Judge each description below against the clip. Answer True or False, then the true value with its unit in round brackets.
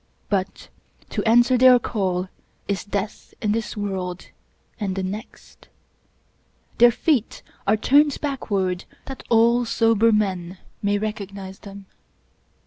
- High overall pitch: True (210 Hz)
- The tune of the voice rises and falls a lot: False (3.4 semitones)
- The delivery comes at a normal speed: False (120 wpm)